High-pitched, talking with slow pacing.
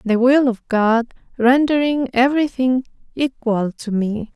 Yes: high, 245 Hz; slow, 125 wpm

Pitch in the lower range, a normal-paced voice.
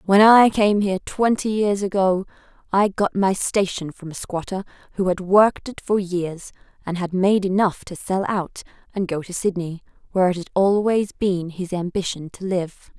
No: high, 190 Hz; average, 185 wpm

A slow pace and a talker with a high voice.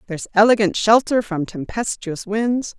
Yes: slow, 130 wpm; high, 205 Hz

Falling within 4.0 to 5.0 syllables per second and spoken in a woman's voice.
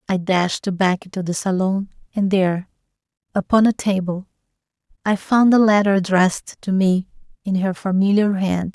Yes: 4.9 syllables/s; female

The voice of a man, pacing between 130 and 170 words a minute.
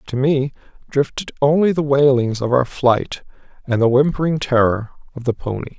Yes: male; average, 165 wpm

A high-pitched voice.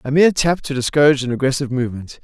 No: low, 135 Hz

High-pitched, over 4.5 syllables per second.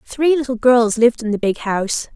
Yes: high, 235 Hz; 5.5 syllables/s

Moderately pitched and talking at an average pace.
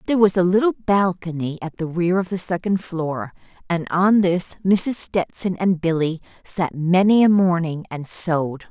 Yes: medium, 180 Hz; average, 170 wpm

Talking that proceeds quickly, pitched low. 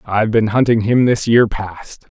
No: average, 190 wpm; low, 110 Hz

